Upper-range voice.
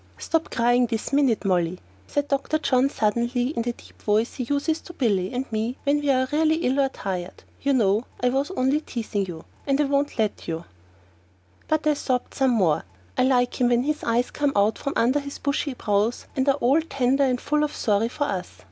Yes: very high, 250 Hz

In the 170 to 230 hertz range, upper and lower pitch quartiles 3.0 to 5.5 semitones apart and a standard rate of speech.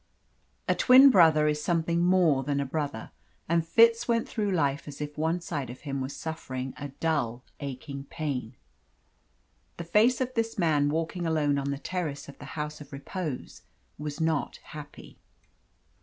No: medium, 150 Hz; average, 3.4 semitones; average, 165 wpm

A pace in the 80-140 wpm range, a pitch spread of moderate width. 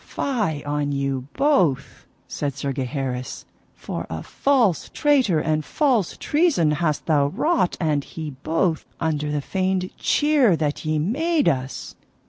No: slow, 135 wpm; wide, 8.4 semitones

